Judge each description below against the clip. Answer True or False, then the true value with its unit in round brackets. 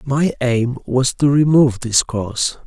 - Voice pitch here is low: True (130 Hz)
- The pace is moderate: True (155 wpm)